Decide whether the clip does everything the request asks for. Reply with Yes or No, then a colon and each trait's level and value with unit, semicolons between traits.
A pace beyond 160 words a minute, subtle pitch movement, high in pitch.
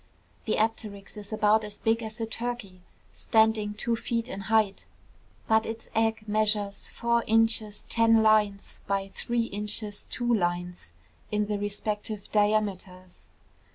No: slow, 135 wpm; narrow, 1.7 semitones; high, 215 Hz